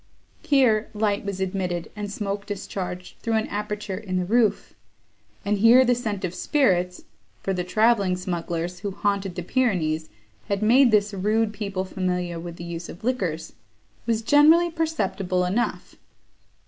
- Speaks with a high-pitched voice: Yes, high, 200 Hz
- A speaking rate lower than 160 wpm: Yes, average, 150 wpm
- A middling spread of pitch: Yes, average, 3.5 semitones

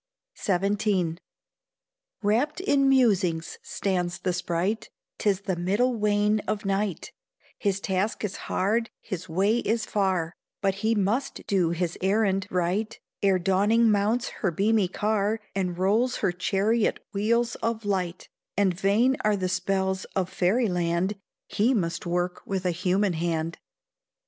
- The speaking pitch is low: No, high, 195 Hz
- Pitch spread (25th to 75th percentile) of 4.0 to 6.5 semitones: No, average, 2.9 semitones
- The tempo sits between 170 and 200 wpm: No, average, 140 wpm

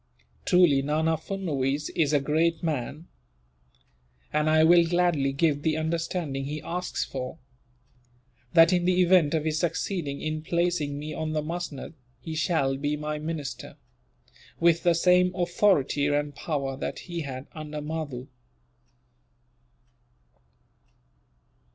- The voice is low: No, medium, 155 Hz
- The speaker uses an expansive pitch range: No, average, 2.8 semitones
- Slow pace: Yes, slow, 125 wpm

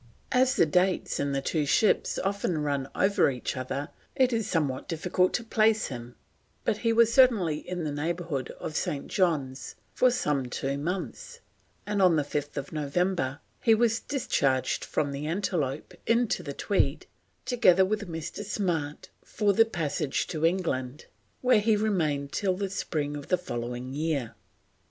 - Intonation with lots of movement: Yes, wide, 6.4 semitones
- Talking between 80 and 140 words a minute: No, average, 155 wpm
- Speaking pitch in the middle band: Yes, medium, 165 Hz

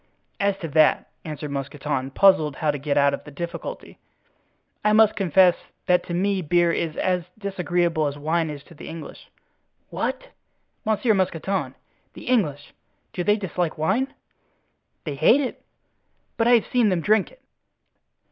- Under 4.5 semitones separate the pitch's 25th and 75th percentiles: No, average, 4.8 semitones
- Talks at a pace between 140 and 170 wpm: Yes, average, 155 wpm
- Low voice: No, medium, 175 Hz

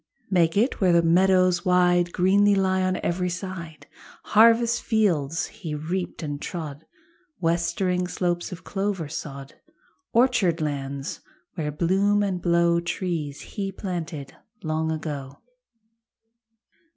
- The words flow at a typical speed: No, slow, 115 wpm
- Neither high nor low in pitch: Yes, medium, 175 Hz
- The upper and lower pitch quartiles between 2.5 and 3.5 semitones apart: Yes, average, 3.0 semitones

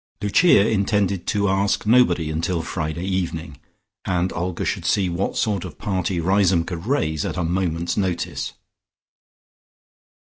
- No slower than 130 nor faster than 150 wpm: Yes, slow, 135 wpm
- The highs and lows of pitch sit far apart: No, average, 2.9 semitones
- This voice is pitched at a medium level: No, very low, 90 Hz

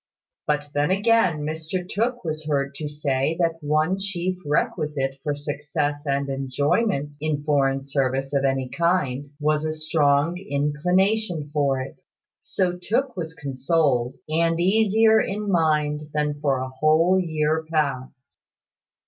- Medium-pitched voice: Yes, medium, 150 Hz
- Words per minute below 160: Yes, slow, 135 wpm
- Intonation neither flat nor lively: Yes, average, 3.4 semitones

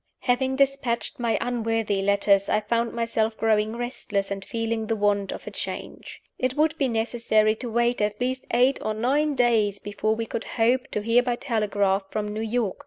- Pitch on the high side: Yes, high, 225 Hz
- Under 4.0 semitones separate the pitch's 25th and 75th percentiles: Yes, narrow, 2.6 semitones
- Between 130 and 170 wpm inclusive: No, average, 185 wpm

